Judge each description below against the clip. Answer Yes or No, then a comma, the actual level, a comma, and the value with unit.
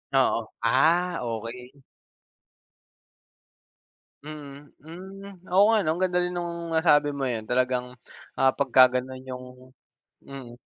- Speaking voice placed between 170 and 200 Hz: No, medium, 140 Hz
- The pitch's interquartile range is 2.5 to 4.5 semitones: No, average, 5.2 semitones